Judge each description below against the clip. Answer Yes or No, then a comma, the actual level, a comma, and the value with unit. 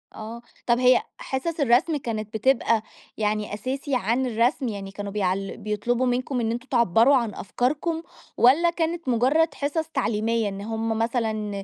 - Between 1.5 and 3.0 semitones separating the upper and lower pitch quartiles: No, average, 3.7 semitones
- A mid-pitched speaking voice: No, high, 235 Hz